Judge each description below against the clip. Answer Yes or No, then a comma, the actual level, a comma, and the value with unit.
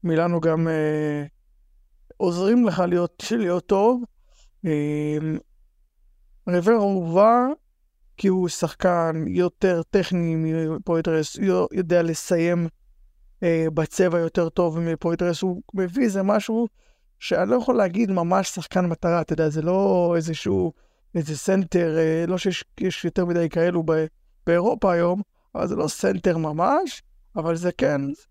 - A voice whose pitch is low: No, medium, 170 Hz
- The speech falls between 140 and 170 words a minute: No, average, 125 wpm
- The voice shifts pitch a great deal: No, average, 2.9 semitones